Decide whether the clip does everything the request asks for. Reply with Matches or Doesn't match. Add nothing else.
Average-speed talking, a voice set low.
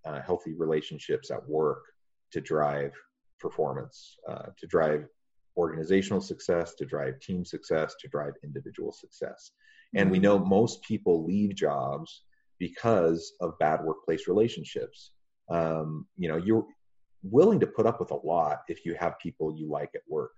Matches